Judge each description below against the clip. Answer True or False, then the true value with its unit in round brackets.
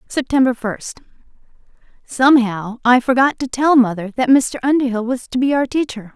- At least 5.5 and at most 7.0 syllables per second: False (5.3 syllables/s)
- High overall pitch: True (250 Hz)